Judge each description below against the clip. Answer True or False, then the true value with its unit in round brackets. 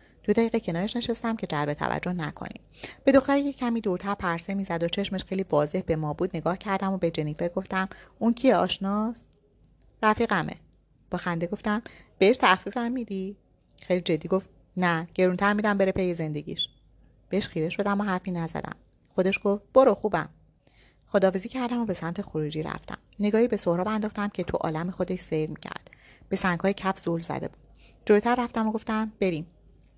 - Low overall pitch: False (190 Hz)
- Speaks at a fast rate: True (170 wpm)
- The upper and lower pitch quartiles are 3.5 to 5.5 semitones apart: True (3.8 semitones)